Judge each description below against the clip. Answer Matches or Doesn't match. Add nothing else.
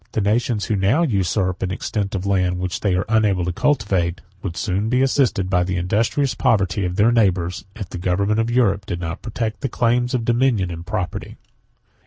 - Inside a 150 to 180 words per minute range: Doesn't match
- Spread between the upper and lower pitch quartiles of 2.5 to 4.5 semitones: Matches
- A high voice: Doesn't match